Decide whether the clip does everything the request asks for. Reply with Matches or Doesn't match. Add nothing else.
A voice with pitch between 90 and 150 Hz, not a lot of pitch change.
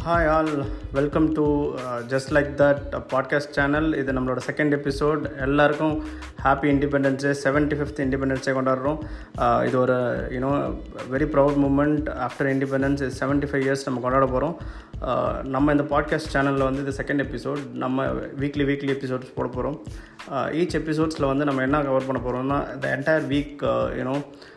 Matches